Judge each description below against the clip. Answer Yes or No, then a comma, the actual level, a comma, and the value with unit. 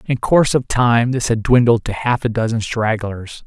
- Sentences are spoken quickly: Yes, fast, 210 wpm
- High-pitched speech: No, low, 120 Hz